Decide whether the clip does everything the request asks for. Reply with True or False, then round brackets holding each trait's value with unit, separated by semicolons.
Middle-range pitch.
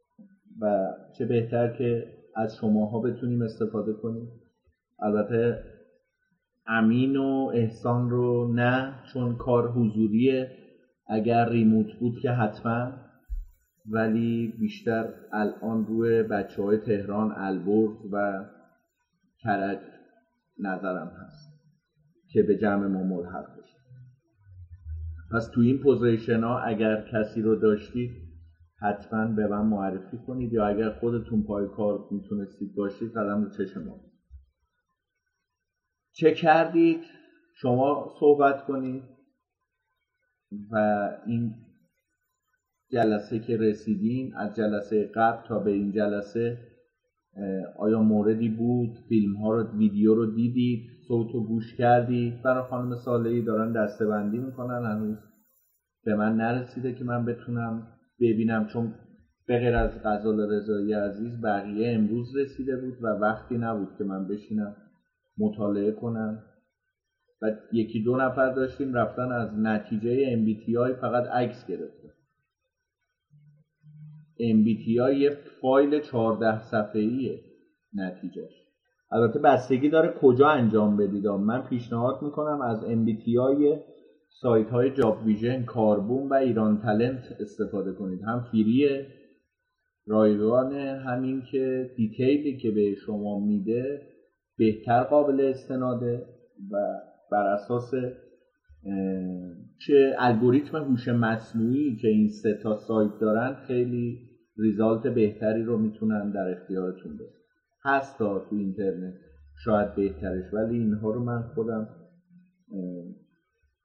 False (115 Hz)